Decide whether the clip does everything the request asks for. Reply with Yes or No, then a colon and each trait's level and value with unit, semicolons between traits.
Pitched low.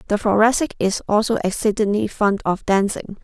No: high, 210 Hz